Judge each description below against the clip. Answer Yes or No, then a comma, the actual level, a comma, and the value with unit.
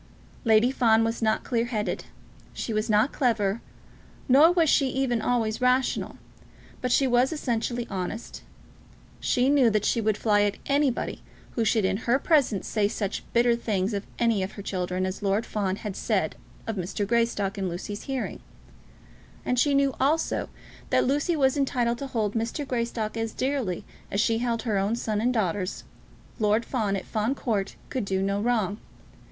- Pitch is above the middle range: Yes, high, 225 Hz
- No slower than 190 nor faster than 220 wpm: No, average, 175 wpm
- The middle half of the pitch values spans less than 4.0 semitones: Yes, average, 3.5 semitones